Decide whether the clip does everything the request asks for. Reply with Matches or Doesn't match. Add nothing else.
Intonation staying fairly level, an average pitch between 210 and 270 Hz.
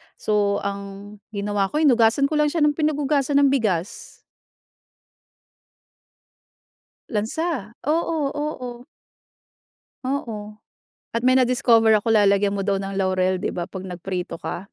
Doesn't match